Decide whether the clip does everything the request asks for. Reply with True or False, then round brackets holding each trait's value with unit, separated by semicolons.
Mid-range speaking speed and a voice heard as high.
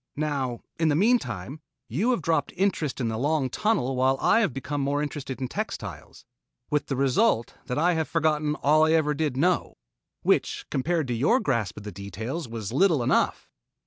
False (185 wpm; 145 Hz)